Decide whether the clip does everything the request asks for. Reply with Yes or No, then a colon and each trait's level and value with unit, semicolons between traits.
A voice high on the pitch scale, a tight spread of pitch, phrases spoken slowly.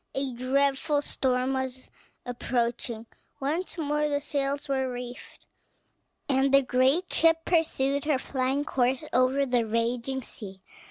Yes: very high, 265 Hz; narrow, 2.2 semitones; slow, 125 wpm